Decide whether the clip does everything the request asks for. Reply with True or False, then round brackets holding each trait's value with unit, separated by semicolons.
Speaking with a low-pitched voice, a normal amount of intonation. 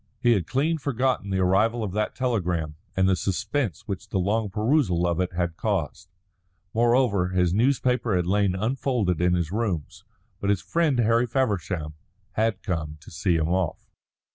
True (100 Hz; 4.8 semitones)